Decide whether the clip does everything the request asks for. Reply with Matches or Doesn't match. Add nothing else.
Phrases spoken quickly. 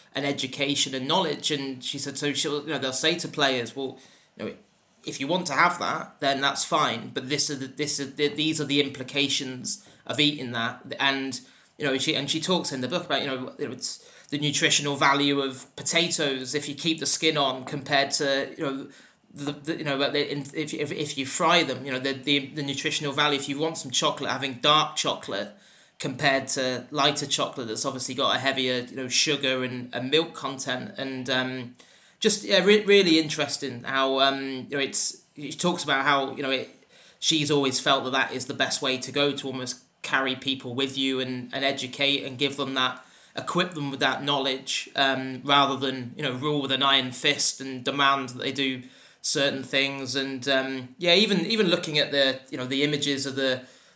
Matches